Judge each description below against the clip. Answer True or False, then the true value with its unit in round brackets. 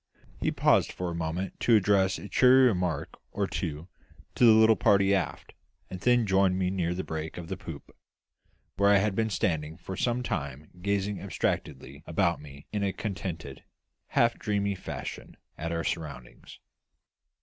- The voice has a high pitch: False (95 Hz)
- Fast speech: False (165 wpm)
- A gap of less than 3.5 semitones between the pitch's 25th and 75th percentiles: False (3.8 semitones)